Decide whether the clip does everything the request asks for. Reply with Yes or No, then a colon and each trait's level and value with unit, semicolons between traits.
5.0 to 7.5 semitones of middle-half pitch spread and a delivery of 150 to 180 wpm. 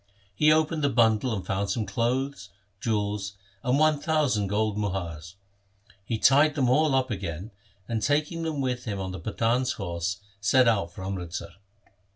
Yes: wide, 5.5 semitones; average, 165 wpm